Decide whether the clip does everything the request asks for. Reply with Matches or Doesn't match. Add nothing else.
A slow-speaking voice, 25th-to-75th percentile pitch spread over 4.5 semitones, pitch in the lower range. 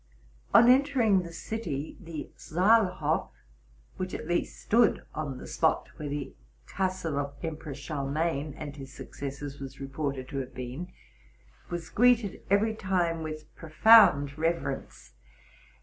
Doesn't match